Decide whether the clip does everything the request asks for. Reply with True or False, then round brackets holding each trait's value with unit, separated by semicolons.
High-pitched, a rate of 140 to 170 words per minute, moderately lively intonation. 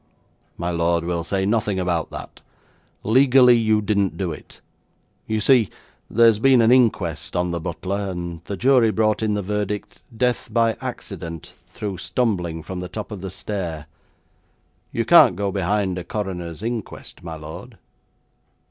False (100 Hz; 155 wpm; 4.0 semitones)